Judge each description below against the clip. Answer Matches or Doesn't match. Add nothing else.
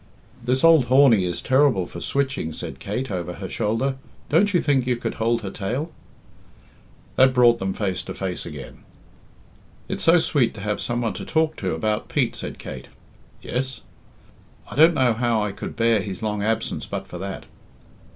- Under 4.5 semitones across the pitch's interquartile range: Doesn't match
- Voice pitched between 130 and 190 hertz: Doesn't match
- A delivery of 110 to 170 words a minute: Doesn't match